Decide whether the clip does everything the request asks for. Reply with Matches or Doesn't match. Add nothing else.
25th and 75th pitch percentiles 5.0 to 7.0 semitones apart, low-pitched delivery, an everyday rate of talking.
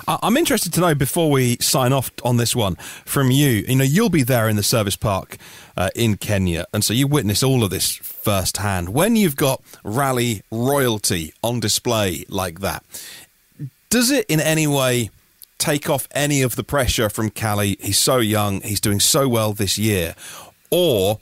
Matches